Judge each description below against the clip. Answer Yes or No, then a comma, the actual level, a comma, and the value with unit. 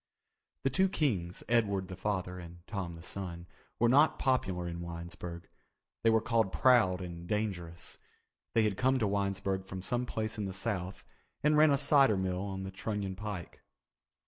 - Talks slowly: No, average, 170 wpm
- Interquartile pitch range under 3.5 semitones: No, average, 4.1 semitones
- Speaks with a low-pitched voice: Yes, low, 100 Hz